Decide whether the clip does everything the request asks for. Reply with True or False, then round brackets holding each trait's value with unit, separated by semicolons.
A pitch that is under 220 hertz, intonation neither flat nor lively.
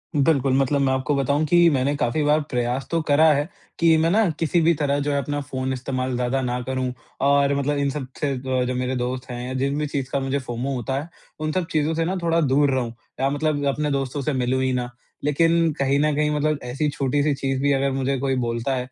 False (140 Hz; 2.3 semitones)